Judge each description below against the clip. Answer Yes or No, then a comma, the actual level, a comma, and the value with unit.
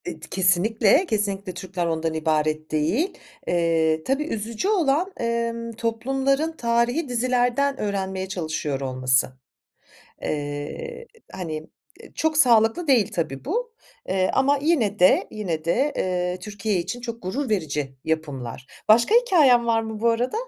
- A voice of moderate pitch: No, high, 215 Hz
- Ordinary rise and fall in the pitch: No, wide, 7.5 semitones